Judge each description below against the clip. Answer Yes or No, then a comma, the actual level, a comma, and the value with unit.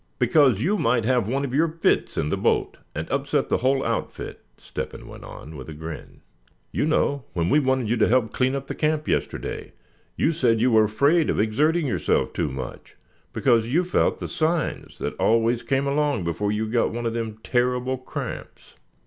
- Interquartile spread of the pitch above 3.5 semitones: Yes, average, 4.5 semitones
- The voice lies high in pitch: No, low, 125 Hz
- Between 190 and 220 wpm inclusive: Yes, average, 200 wpm